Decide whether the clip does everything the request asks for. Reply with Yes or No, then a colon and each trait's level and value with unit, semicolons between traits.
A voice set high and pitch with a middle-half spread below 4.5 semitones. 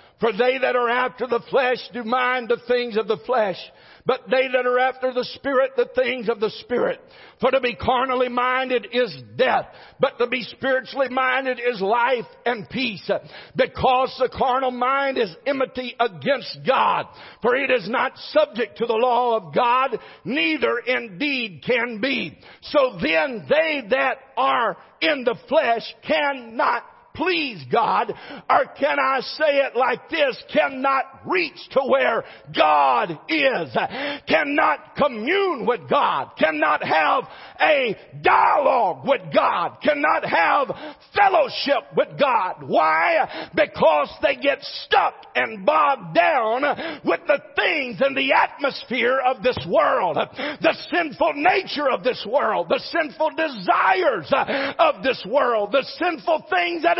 Yes: very high, 260 Hz; average, 3.8 semitones